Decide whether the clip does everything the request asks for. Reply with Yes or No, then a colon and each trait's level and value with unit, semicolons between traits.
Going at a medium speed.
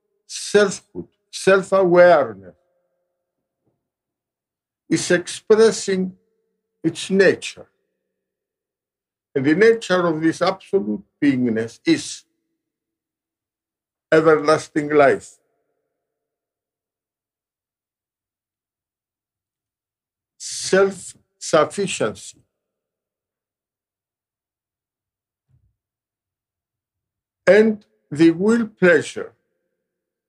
No: slow, 45 wpm